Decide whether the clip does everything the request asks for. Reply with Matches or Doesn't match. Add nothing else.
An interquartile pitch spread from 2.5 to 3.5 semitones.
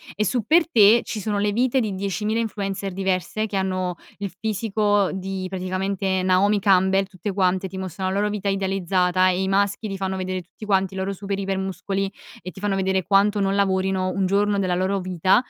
Doesn't match